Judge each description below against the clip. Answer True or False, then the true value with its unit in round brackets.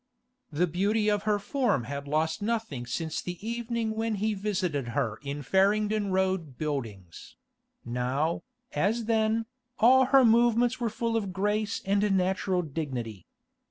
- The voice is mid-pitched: False (195 Hz)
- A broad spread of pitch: True (6.9 semitones)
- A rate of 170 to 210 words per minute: False (140 wpm)